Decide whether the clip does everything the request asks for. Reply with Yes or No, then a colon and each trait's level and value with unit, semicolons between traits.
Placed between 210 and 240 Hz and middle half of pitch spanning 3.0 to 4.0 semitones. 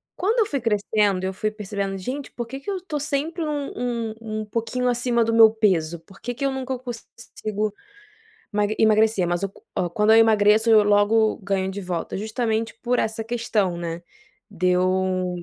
Yes: high, 220 Hz; average, 3.7 semitones